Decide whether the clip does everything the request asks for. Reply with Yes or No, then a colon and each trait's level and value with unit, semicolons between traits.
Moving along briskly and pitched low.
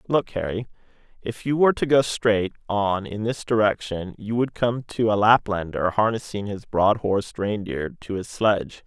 No: average, 175 wpm; low, 105 Hz